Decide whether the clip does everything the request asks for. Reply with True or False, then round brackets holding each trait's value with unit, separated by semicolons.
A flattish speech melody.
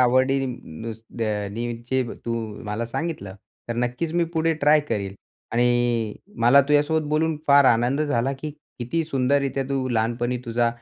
False (3.7 semitones)